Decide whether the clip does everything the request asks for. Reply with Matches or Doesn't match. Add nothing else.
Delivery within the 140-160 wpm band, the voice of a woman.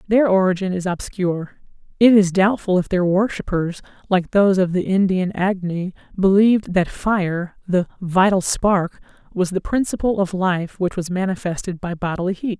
Matches